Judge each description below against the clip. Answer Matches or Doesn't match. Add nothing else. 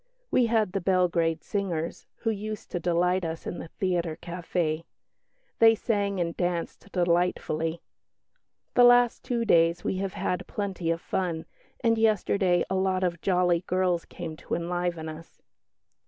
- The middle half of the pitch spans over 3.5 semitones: Doesn't match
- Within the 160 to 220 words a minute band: Doesn't match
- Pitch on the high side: Doesn't match